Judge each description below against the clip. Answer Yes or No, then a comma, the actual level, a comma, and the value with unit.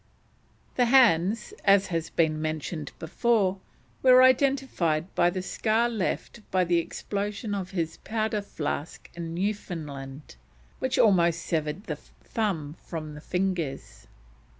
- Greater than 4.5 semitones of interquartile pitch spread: Yes, average, 5.0 semitones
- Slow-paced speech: Yes, slow, 125 wpm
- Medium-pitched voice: Yes, medium, 180 Hz